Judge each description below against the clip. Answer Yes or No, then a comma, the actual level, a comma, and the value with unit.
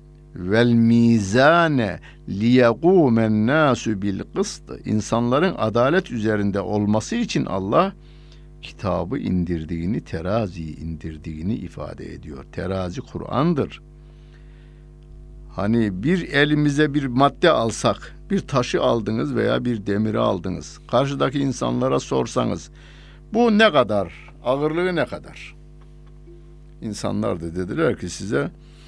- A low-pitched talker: Yes, low, 120 Hz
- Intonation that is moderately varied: No, wide, 7.3 semitones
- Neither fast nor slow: No, slow, 90 wpm